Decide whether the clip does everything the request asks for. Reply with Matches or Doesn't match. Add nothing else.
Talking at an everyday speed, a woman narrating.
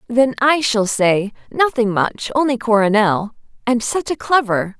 Matches